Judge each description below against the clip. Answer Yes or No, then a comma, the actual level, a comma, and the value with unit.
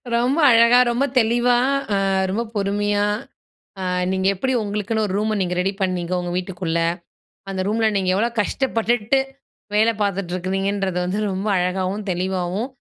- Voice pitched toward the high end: Yes, high, 200 Hz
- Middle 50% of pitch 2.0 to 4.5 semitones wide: Yes, average, 3.3 semitones